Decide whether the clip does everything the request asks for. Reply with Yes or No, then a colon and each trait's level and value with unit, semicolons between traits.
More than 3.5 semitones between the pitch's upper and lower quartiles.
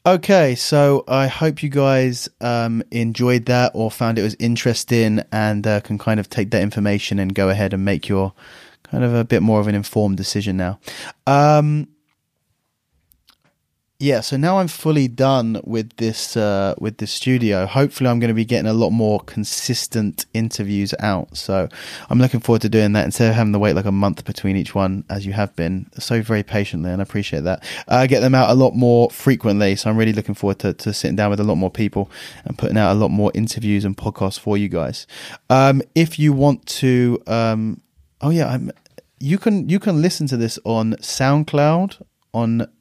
Yes: average, 4.0 semitones